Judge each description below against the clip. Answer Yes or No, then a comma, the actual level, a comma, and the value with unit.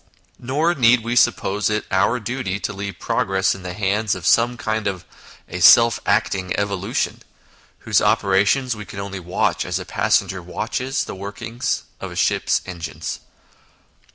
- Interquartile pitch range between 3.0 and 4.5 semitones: Yes, average, 3.8 semitones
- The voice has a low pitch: Yes, low, 105 Hz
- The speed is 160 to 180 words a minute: Yes, average, 170 wpm